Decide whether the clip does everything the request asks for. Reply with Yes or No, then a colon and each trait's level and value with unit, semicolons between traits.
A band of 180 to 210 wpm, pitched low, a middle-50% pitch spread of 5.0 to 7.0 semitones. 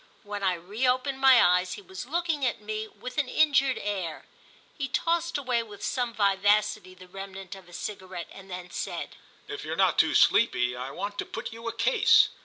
No: average, 195 wpm; high, 210 Hz; wide, 5.5 semitones